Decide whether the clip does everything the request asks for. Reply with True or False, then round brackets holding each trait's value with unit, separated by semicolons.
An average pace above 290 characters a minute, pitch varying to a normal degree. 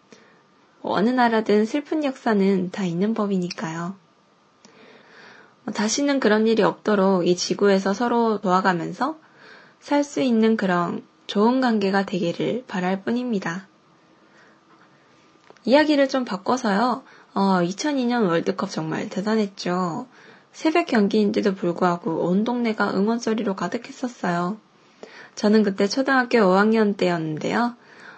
False (260 characters per minute; 4.2 semitones)